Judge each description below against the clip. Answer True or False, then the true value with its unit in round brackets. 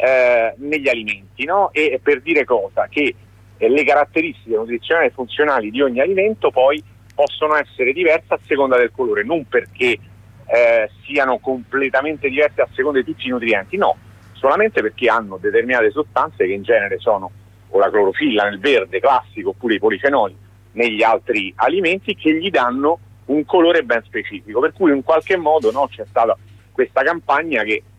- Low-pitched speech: False (150 Hz)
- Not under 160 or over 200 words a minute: True (170 wpm)